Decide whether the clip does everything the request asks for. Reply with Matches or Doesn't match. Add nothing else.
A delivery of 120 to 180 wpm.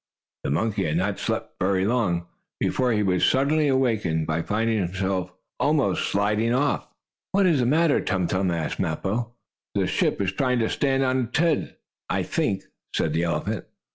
Matches